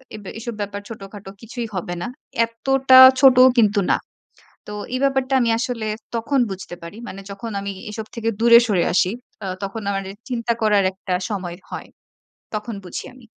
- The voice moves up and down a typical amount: Yes, average, 3.2 semitones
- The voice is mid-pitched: No, high, 220 Hz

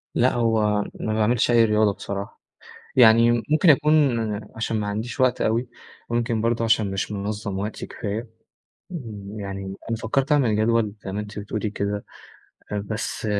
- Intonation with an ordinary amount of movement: No, narrow, 2.2 semitones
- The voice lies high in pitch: No, low, 110 Hz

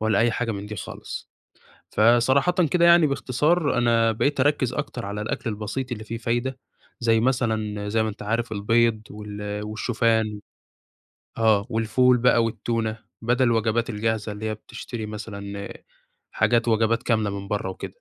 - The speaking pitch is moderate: No, low, 115 Hz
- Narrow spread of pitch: Yes, narrow, 2.2 semitones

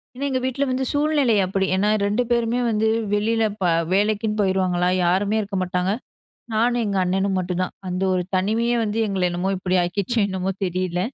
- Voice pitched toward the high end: Yes, high, 200 Hz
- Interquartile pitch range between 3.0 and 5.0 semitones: Yes, average, 3.6 semitones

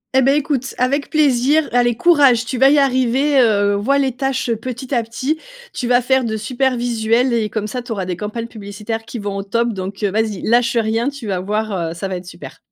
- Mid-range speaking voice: No, high, 235 Hz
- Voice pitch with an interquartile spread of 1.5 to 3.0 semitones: No, average, 3.6 semitones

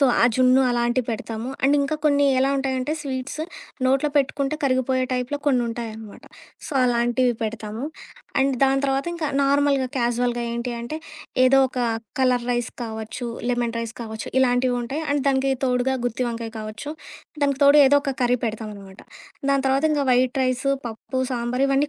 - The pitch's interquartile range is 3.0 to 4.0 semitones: No, narrow, 2.4 semitones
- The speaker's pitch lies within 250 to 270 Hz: Yes, very high, 255 Hz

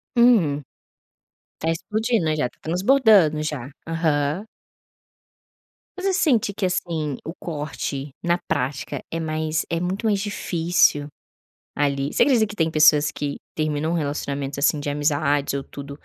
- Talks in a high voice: No, medium, 155 Hz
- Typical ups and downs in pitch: Yes, average, 4.2 semitones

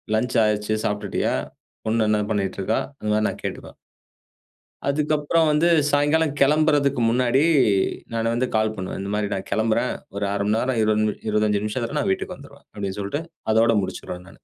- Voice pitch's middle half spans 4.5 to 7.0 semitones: Yes, average, 5.2 semitones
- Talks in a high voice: No, low, 110 Hz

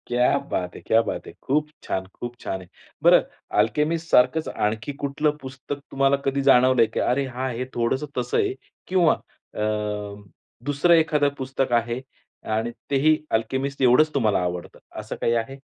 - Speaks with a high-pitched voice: No, low, 130 Hz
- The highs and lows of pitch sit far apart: No, average, 3.7 semitones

